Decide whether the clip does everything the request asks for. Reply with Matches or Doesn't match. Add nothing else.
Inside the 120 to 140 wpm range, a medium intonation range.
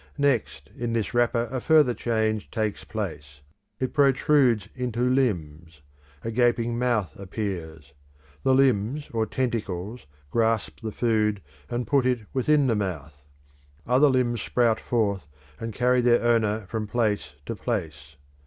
Matches